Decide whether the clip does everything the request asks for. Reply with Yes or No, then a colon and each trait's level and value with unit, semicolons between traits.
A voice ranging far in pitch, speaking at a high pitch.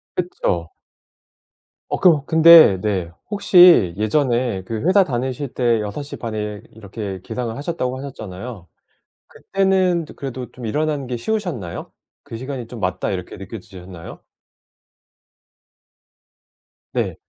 No: wide, 6.8 semitones; low, 120 Hz